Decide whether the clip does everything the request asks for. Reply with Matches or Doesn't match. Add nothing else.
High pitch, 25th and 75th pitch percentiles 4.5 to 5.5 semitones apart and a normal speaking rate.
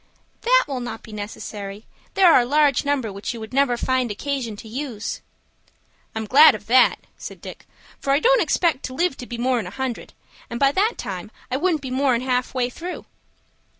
Doesn't match